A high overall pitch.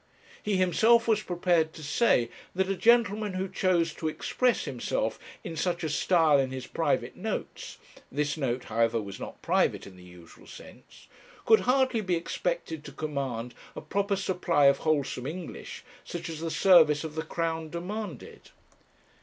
No: medium, 165 Hz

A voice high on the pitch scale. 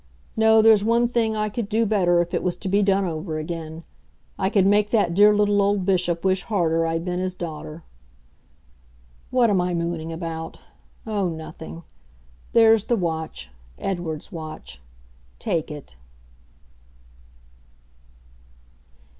No: medium, 180 Hz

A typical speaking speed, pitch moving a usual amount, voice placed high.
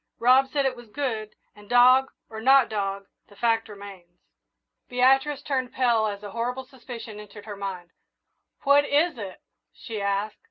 Yes: average, 160 wpm; average, 4.2 semitones; high, 230 Hz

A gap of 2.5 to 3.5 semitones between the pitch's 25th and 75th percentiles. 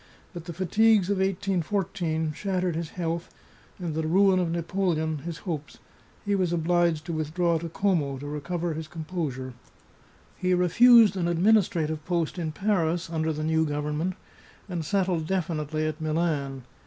Yes: average, 2.8 semitones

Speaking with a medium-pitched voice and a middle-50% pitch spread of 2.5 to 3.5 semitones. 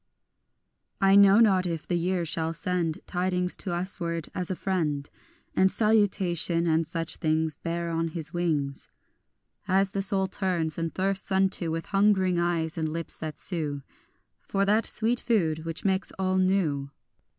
Yes: medium, 175 Hz; average, 2.8 semitones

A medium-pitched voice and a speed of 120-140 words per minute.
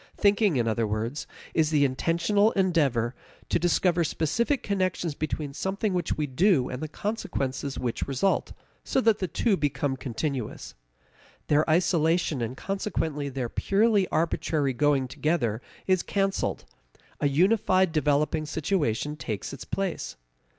Yes: medium, 155 Hz; slow, 135 wpm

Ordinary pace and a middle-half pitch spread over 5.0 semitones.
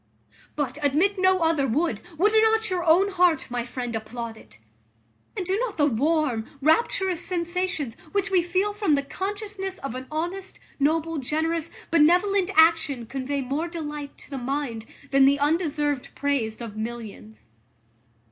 Yes: average, 150 wpm; wide, 5.4 semitones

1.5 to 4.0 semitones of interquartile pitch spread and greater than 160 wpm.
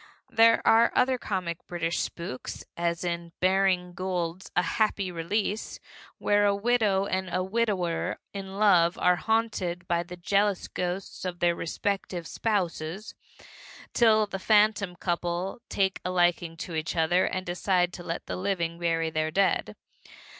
No: average, 2.7 semitones; average, 145 wpm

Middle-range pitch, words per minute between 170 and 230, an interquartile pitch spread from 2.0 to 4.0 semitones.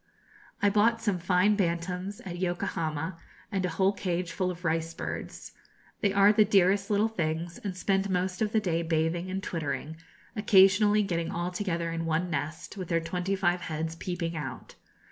Yes: medium, 180 Hz; average, 175 wpm; average, 2.9 semitones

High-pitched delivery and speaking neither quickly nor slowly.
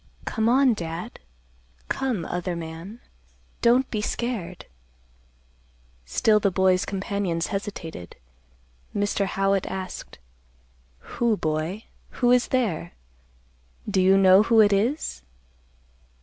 No: high, 195 Hz; slow, 105 wpm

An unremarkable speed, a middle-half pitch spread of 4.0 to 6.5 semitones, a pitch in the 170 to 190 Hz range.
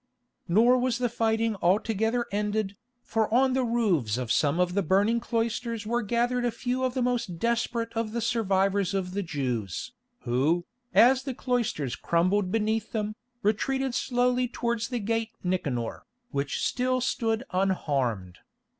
No: average, 150 wpm; average, 4.8 semitones; high, 220 Hz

